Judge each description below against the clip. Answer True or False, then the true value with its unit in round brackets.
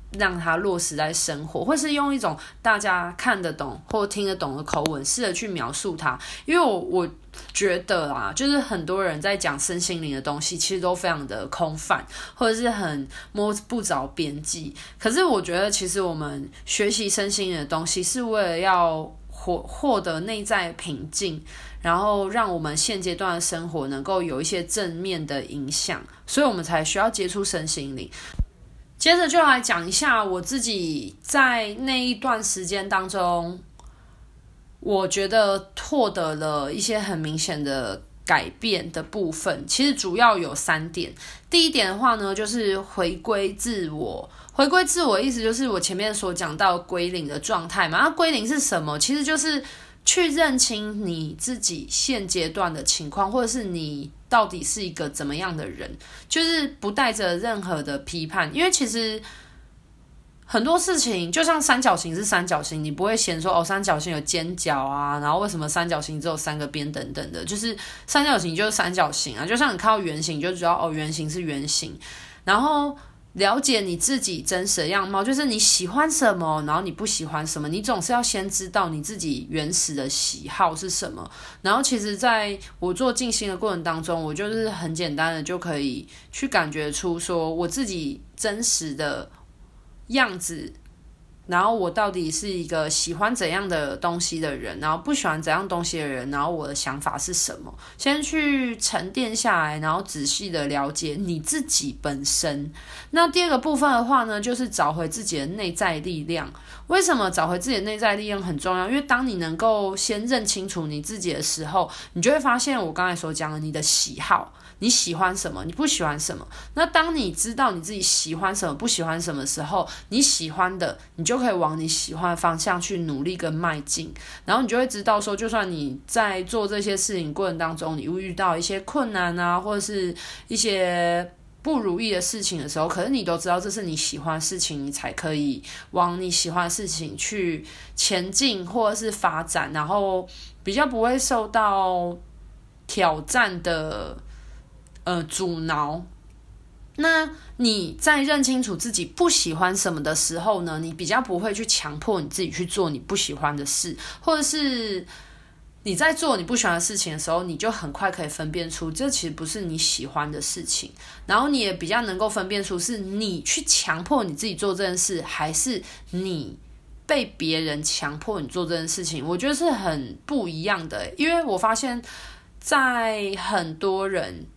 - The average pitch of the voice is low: False (185 Hz)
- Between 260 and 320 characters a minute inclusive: True (275 characters per minute)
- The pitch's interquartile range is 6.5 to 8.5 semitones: False (5.5 semitones)